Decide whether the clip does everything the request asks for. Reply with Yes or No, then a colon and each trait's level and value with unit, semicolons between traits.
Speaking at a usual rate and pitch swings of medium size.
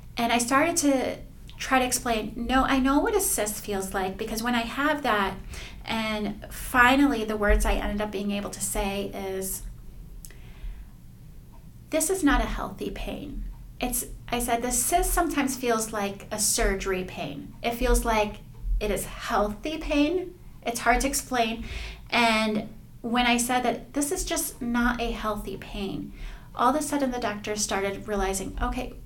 Yes: average, 165 wpm; average, 4.0 semitones